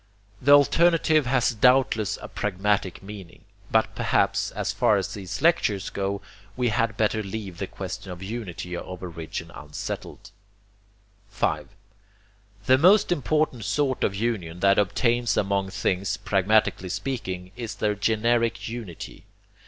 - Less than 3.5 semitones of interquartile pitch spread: No, average, 4.3 semitones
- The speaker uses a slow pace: Yes, slow, 130 wpm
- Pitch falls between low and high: No, low, 105 Hz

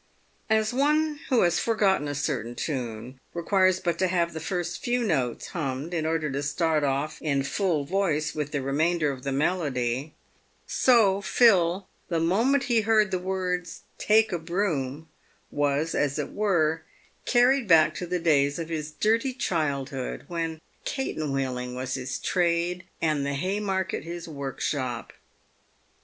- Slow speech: No, average, 155 wpm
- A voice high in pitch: No, medium, 165 Hz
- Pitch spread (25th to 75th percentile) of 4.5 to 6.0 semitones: Yes, average, 5.1 semitones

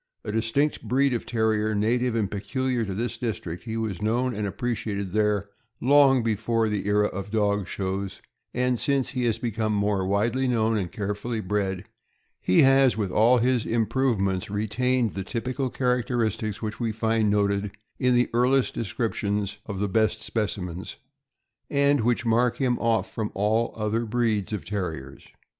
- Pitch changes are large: No, average, 3.1 semitones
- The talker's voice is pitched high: No, low, 110 Hz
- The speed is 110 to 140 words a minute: No, average, 160 wpm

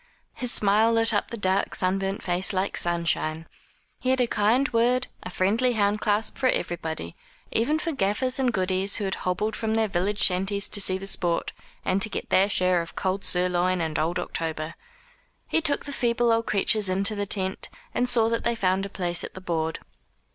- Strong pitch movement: No, average, 3.7 semitones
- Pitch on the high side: Yes, high, 200 Hz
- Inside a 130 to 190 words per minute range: No, average, 200 wpm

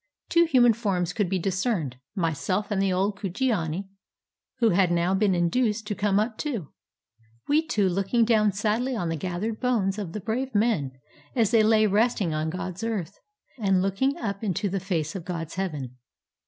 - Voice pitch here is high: Yes, high, 195 Hz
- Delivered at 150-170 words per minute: No, average, 180 wpm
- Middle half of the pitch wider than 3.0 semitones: Yes, average, 3.8 semitones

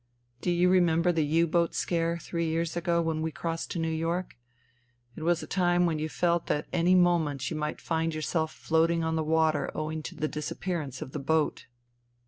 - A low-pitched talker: No, medium, 165 Hz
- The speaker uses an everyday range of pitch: No, narrow, 1.6 semitones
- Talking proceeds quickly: Yes, fast, 210 wpm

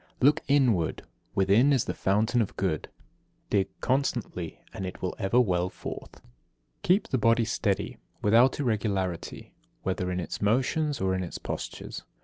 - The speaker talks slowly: No, average, 155 wpm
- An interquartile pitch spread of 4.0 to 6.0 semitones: Yes, average, 5.1 semitones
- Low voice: Yes, low, 105 Hz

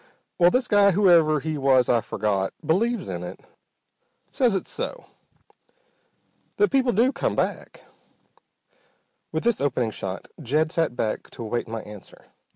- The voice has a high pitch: No, medium, 155 Hz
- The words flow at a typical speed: Yes, average, 145 wpm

